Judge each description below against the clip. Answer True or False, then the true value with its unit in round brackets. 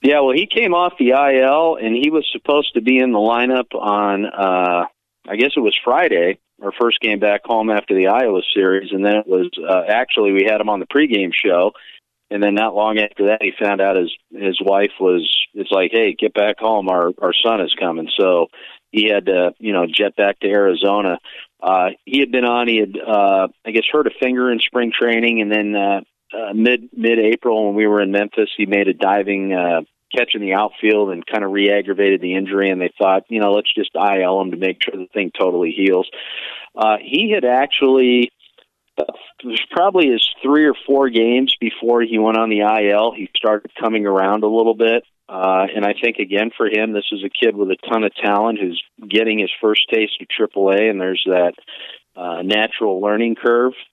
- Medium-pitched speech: False (105 Hz)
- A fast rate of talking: True (215 wpm)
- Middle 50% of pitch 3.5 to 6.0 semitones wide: False (3.0 semitones)